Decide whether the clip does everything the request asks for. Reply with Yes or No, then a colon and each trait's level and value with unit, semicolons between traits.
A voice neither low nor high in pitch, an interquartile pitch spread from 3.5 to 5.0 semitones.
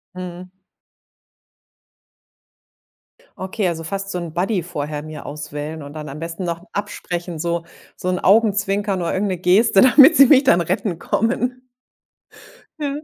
Yes: medium, 180 Hz; average, 3.8 semitones